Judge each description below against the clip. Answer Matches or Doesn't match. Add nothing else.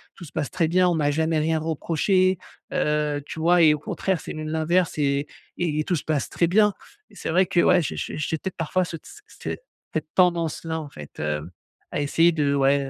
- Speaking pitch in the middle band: Matches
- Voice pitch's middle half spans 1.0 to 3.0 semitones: Matches